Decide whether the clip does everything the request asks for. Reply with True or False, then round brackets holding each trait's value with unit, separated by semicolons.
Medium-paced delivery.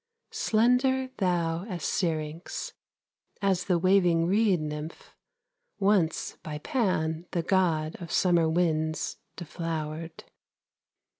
False (95 wpm)